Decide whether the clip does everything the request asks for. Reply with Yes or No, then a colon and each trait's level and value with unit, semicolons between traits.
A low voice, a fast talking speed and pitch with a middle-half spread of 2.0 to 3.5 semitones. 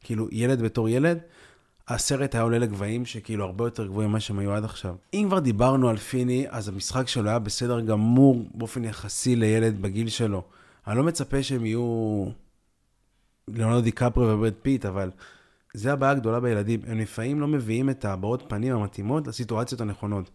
Yes: low, 115 Hz; fast, 170 wpm; average, 3.0 semitones